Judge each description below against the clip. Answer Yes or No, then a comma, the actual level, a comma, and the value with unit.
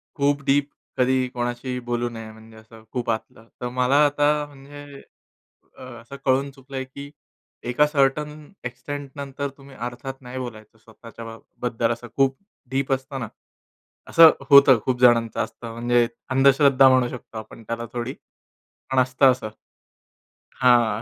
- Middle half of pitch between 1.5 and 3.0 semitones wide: Yes, average, 2.7 semitones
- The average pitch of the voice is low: Yes, low, 130 Hz